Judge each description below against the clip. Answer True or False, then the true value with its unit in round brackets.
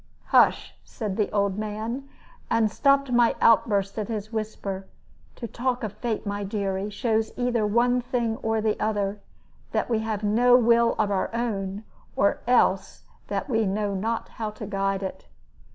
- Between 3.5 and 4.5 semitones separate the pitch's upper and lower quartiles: False (2.6 semitones)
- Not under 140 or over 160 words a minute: False (170 wpm)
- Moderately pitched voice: False (215 Hz)